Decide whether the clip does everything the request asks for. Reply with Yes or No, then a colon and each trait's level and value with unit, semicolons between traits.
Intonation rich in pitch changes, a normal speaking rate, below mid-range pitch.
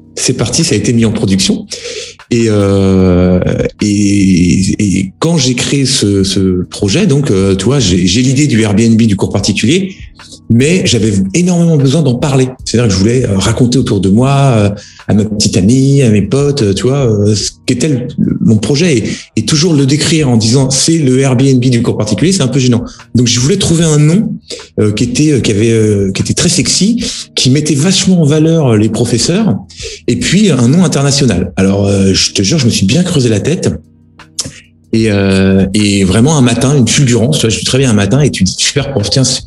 Yes: wide, 5.7 semitones; average, 195 wpm; low, 120 Hz